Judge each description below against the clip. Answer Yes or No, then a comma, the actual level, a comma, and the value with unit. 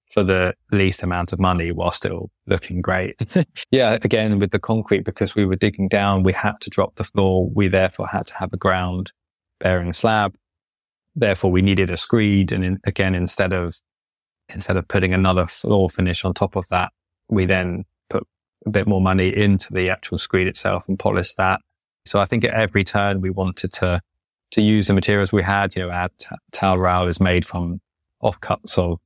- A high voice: No, very low, 95 Hz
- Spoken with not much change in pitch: Yes, narrow, 1.9 semitones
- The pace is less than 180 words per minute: No, average, 195 wpm